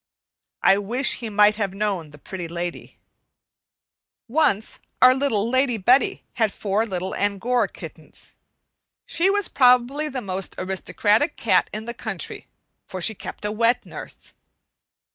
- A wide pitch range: No, average, 4.4 semitones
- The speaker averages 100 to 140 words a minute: Yes, slow, 135 wpm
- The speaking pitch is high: Yes, high, 215 Hz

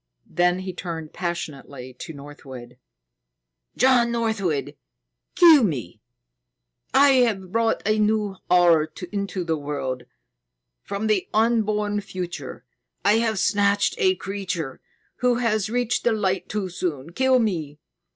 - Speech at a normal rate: No, slow, 120 wpm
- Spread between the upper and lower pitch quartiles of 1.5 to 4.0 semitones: No, average, 5.3 semitones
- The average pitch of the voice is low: No, high, 195 Hz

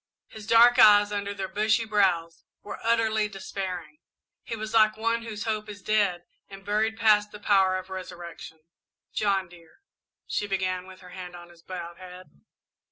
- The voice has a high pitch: Yes, high, 200 Hz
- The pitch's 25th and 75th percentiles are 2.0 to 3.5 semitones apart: Yes, average, 2.8 semitones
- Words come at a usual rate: Yes, average, 170 wpm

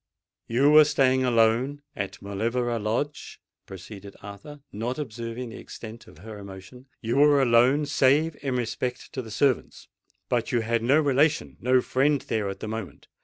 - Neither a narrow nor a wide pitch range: Yes, average, 4.0 semitones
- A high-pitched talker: No, low, 120 Hz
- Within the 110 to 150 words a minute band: No, average, 160 wpm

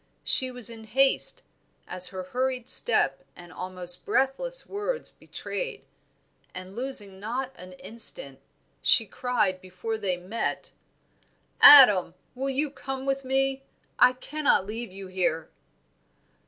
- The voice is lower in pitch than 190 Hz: No, high, 230 Hz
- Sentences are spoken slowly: Yes, slow, 125 wpm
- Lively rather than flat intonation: Yes, wide, 6.4 semitones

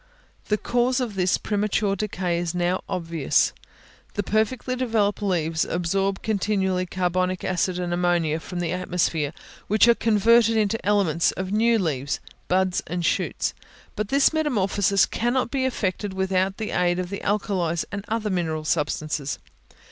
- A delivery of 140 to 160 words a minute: Yes, average, 150 wpm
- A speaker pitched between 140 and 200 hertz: Yes, high, 190 Hz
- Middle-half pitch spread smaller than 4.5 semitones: Yes, average, 3.3 semitones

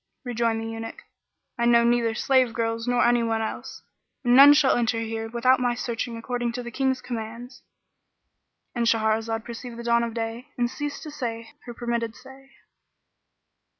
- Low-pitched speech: No, high, 235 Hz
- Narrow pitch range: Yes, narrow, 1.5 semitones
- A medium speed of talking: Yes, average, 160 wpm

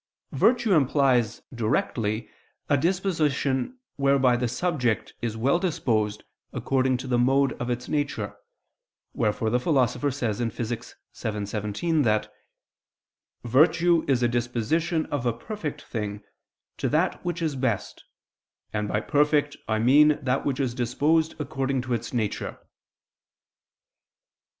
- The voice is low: Yes, low, 130 Hz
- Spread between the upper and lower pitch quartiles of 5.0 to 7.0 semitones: No, average, 4.2 semitones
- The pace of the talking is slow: Yes, slow, 130 wpm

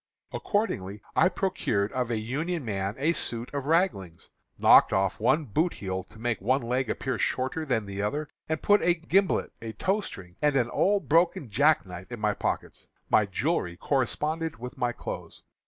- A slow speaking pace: No, average, 180 wpm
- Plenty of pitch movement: Yes, wide, 7.2 semitones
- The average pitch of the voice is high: No, low, 125 Hz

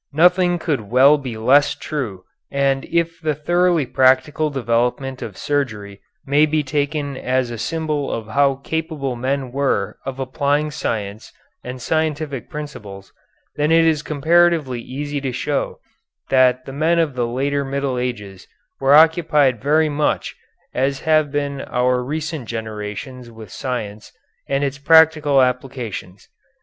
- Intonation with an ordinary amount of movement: Yes, average, 3.2 semitones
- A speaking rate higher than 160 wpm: No, average, 140 wpm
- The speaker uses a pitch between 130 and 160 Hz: Yes, medium, 140 Hz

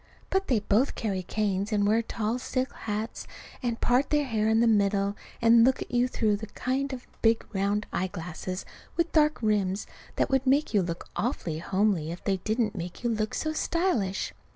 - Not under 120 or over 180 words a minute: No, average, 190 wpm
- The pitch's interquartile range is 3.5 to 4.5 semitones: Yes, average, 3.9 semitones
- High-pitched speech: Yes, high, 220 Hz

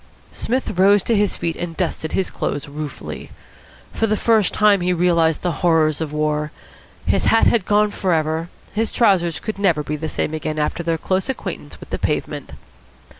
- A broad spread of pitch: No, average, 4.6 semitones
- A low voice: No, medium, 175 Hz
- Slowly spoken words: No, average, 185 wpm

